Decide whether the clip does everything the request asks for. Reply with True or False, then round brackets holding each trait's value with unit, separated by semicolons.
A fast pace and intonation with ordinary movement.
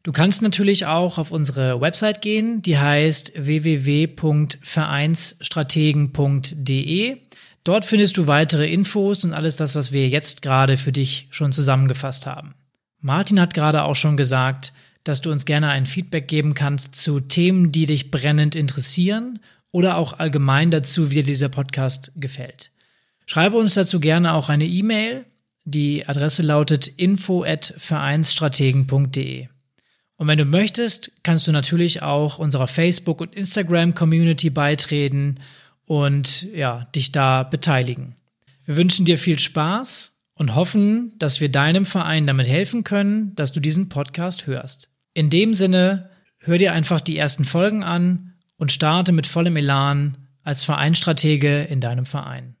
False (145 wpm; 3.7 semitones)